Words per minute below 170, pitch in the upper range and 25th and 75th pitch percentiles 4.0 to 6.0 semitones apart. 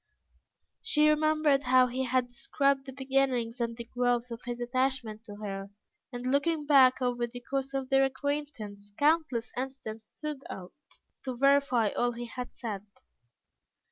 No: average, 150 wpm; very high, 255 Hz; narrow, 2.5 semitones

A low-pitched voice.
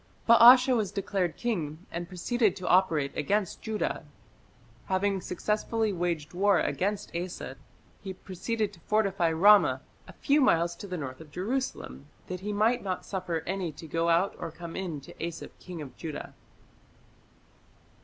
No: medium, 185 Hz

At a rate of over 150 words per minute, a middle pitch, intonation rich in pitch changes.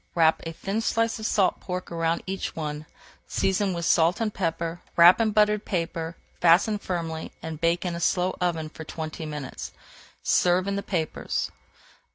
No: average, 170 wpm; medium, 175 Hz; average, 3.0 semitones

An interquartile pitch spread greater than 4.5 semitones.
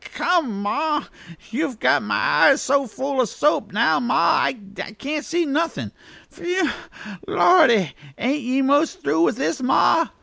Yes: average, 5.1 semitones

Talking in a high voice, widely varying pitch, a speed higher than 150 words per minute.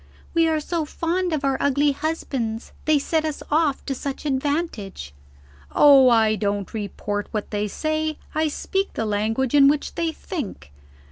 Yes: very high, 280 Hz; wide, 6.1 semitones; average, 160 wpm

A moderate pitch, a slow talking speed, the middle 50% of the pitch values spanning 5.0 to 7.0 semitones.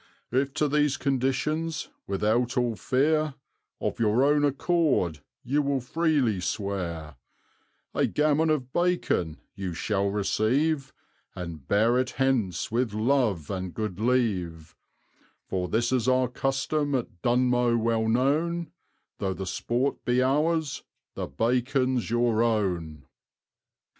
No: low, 125 Hz; slow, 125 wpm; wide, 5.5 semitones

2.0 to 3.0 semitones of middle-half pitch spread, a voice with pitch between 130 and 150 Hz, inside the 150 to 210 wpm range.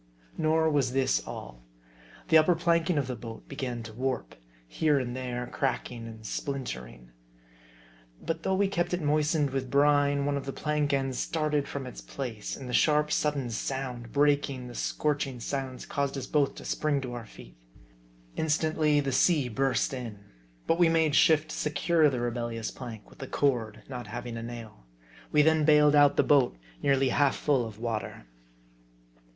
No: average, 3.6 semitones; low, 135 Hz; average, 175 wpm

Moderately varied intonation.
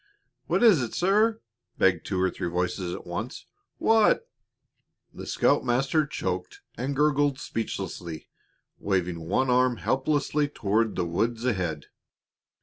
No: wide, 8.0 semitones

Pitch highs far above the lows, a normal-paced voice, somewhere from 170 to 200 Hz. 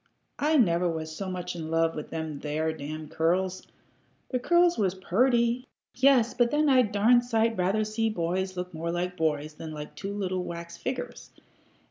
Yes: wide, 6.4 semitones; average, 180 wpm; medium, 185 Hz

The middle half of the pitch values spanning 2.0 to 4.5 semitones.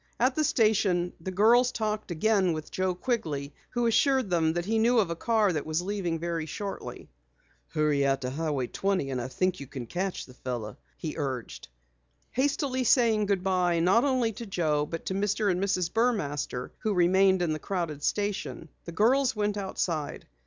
No: wide, 5.5 semitones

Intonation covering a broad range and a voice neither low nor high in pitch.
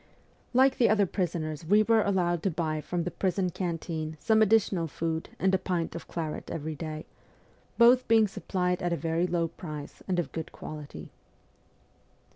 No: average, 3.4 semitones; medium, 175 Hz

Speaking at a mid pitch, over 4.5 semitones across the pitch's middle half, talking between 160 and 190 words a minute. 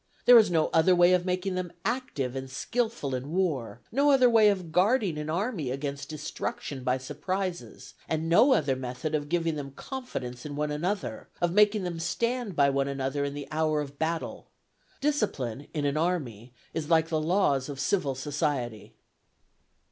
Yes: medium, 155 Hz; average, 5.0 semitones; average, 175 wpm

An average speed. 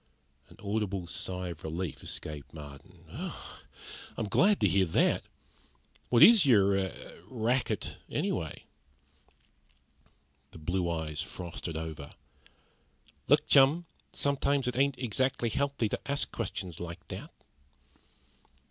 No: slow, 115 wpm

